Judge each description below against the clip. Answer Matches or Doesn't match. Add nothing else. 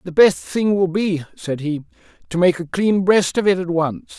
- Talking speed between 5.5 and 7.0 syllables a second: Doesn't match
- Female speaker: Doesn't match